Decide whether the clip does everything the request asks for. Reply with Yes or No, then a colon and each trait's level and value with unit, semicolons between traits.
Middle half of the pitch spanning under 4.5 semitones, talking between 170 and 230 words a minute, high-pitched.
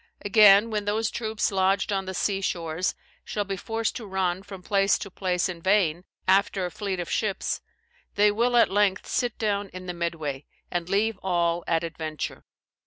Yes: average, 2.8 semitones; average, 180 wpm; high, 195 Hz